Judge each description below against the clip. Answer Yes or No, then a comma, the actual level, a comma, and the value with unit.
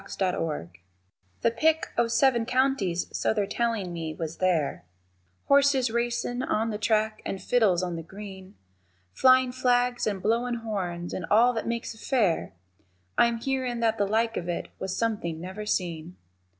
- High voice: Yes, high, 220 Hz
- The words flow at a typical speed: Yes, average, 165 wpm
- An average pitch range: Yes, average, 4.6 semitones